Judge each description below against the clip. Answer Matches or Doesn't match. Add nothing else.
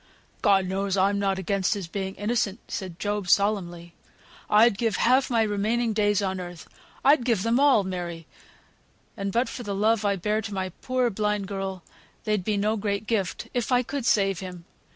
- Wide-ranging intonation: Doesn't match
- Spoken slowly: Doesn't match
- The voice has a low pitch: Doesn't match